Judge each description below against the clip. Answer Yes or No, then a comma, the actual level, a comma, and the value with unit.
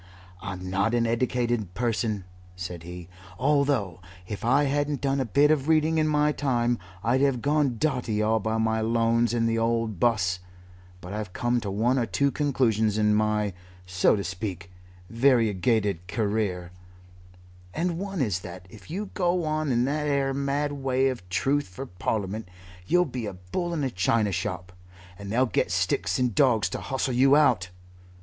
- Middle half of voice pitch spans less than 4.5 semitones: No, average, 5.3 semitones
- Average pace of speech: Yes, average, 170 wpm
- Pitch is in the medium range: No, low, 115 Hz